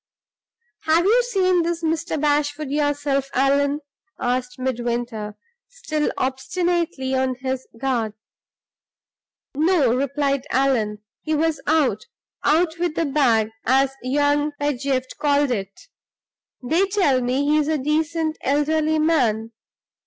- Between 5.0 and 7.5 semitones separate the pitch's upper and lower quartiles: No, average, 3.4 semitones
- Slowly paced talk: Yes, slow, 115 wpm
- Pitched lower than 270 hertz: No, very high, 285 Hz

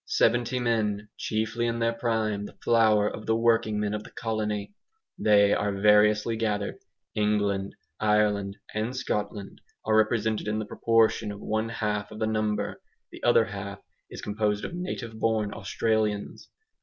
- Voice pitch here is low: Yes, low, 110 Hz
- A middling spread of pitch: No, narrow, 1.4 semitones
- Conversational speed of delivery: Yes, average, 155 wpm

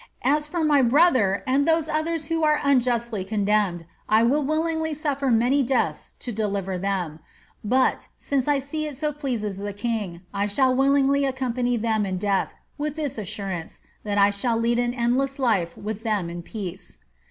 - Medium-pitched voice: No, high, 245 Hz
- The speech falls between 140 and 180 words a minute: Yes, average, 175 wpm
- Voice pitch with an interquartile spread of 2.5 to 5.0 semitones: No, wide, 5.6 semitones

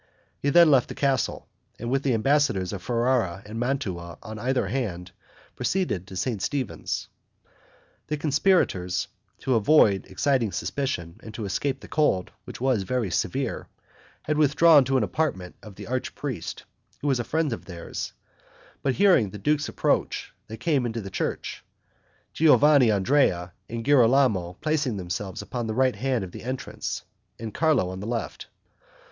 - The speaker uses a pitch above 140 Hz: No, low, 120 Hz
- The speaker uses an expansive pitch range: Yes, wide, 6.2 semitones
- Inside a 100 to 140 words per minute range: No, average, 155 wpm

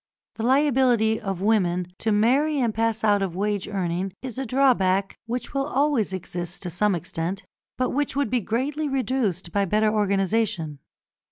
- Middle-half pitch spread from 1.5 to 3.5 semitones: No, average, 5.0 semitones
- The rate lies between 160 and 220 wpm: Yes, average, 165 wpm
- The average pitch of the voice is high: Yes, high, 215 Hz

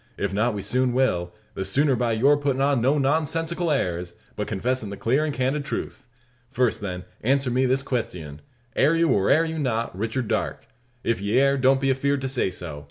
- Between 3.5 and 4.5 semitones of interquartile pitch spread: No, average, 4.9 semitones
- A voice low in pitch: Yes, low, 130 Hz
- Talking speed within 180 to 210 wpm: Yes, fast, 205 wpm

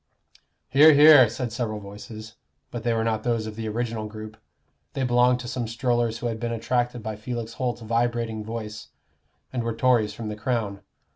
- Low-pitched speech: Yes, low, 115 Hz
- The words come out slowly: No, average, 185 wpm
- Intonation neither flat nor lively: No, narrow, 2.0 semitones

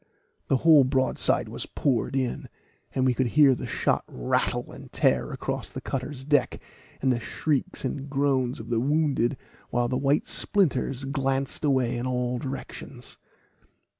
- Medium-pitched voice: No, low, 130 Hz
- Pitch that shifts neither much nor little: No, narrow, 1.9 semitones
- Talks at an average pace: Yes, average, 155 wpm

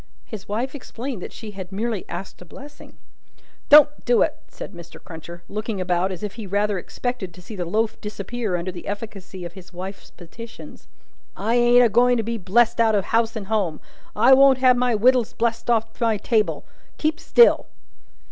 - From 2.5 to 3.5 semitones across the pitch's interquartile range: No, average, 4.1 semitones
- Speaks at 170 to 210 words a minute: Yes, average, 190 wpm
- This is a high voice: Yes, high, 220 Hz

